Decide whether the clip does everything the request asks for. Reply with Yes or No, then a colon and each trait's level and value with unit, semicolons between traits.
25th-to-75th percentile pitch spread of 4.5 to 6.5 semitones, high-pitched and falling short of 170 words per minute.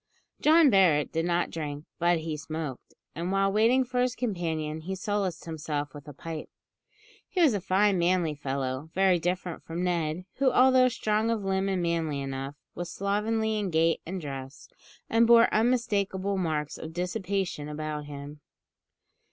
No: average, 5.0 semitones; medium, 175 Hz; average, 160 wpm